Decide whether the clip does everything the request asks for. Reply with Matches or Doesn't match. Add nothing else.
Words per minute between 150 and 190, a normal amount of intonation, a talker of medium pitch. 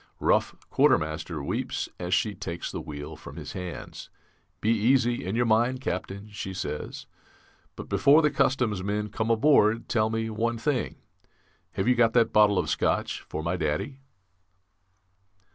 Doesn't match